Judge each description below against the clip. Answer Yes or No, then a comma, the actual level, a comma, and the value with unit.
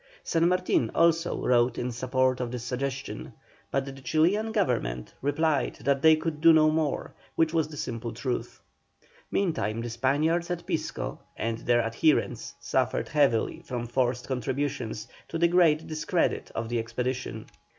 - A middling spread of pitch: Yes, average, 4.9 semitones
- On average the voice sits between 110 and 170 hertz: Yes, low, 135 Hz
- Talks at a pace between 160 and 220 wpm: No, average, 150 wpm